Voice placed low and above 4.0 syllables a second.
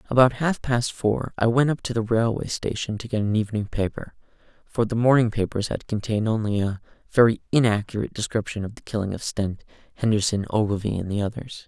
Yes: low, 110 Hz; 6.0 syllables/s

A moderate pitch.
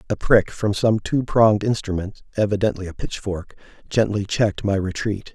No: low, 105 Hz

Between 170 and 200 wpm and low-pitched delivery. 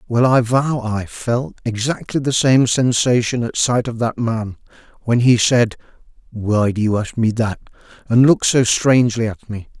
Yes: average, 180 wpm; low, 120 Hz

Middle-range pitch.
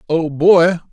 Yes: medium, 165 Hz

